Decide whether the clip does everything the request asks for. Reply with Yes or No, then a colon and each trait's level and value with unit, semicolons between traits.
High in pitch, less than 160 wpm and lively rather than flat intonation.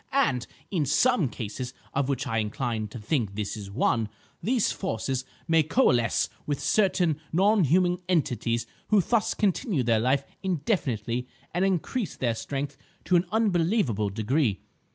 No: medium, 140 Hz; slow, 135 wpm; wide, 8.0 semitones